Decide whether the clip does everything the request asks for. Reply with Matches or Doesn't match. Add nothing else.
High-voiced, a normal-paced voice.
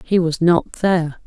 Doesn't match